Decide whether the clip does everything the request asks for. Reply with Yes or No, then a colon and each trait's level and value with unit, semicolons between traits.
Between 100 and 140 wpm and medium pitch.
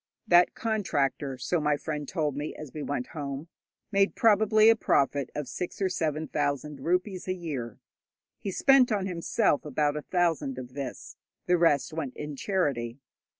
No: average, 165 wpm; medium, 155 Hz